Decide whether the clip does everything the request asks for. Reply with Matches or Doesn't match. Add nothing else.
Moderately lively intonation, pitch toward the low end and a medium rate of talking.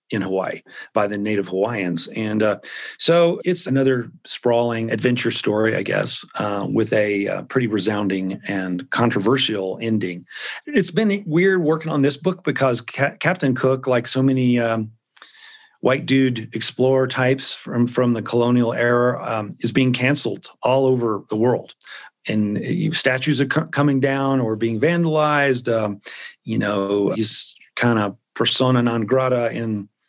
Matches